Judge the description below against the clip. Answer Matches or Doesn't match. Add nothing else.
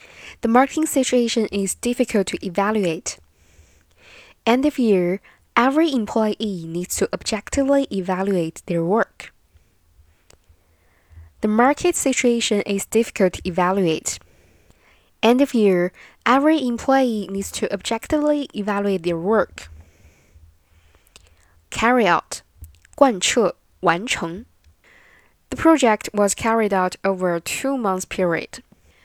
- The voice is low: Doesn't match